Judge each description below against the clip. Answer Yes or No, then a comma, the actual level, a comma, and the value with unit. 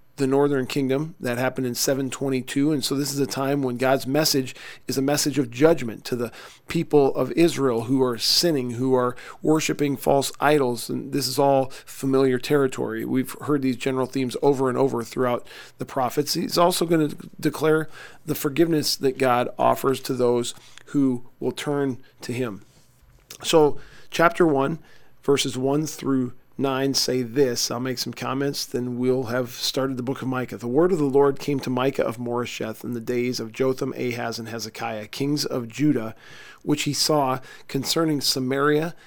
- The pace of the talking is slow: No, average, 175 wpm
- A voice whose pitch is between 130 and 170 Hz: Yes, low, 135 Hz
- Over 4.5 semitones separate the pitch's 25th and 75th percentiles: No, narrow, 2.5 semitones